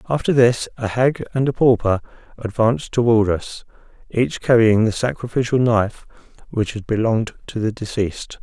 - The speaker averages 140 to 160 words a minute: Yes, average, 150 wpm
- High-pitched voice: No, low, 115 Hz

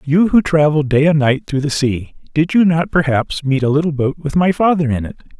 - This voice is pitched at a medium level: Yes, medium, 150 Hz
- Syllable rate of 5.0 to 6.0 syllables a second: Yes, 5.3 syllables/s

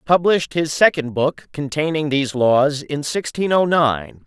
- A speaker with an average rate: Yes, average, 155 wpm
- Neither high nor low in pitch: Yes, medium, 150 Hz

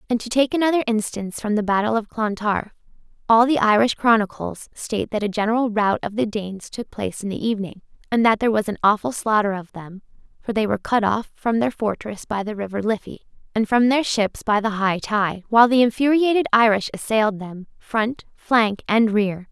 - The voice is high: Yes, high, 220 Hz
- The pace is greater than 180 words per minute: Yes, average, 200 wpm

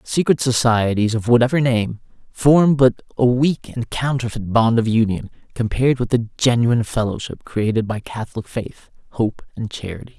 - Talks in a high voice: No, low, 120 Hz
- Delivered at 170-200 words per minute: No, average, 155 wpm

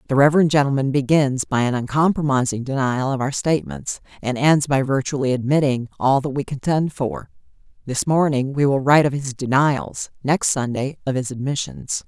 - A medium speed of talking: Yes, average, 170 wpm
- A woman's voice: Yes, female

